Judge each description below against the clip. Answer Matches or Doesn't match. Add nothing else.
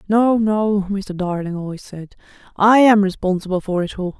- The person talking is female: Matches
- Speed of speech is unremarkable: Matches